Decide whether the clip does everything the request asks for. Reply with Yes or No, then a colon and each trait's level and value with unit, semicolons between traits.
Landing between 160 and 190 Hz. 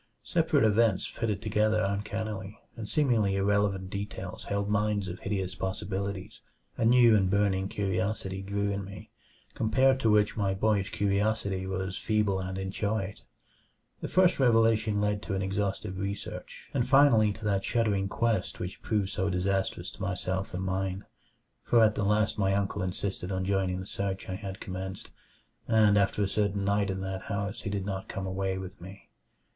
No: low, 100 Hz